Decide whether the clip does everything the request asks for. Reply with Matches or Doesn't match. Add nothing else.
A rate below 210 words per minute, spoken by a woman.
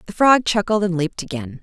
Doesn't match